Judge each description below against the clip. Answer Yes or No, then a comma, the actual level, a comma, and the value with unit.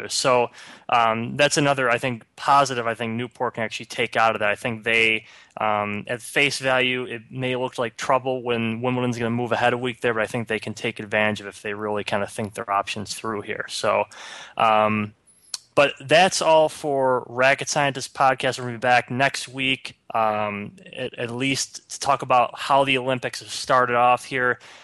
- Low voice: Yes, low, 120 Hz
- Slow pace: No, fast, 205 wpm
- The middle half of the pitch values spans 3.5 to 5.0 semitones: No, average, 2.8 semitones